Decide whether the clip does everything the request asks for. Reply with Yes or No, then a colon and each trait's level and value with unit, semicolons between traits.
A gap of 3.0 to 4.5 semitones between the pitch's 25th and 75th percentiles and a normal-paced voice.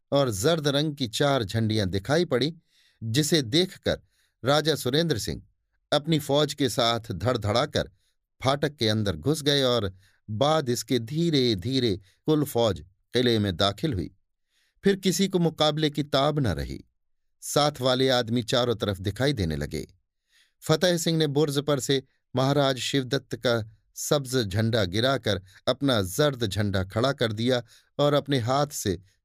No: average, 5.1 semitones; average, 150 wpm